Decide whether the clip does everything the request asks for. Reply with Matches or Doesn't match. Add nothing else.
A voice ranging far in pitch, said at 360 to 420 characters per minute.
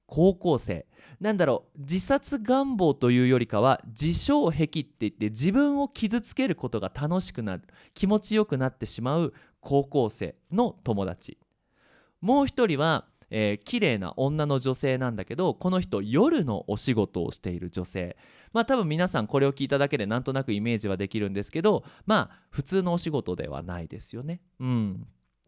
Doesn't match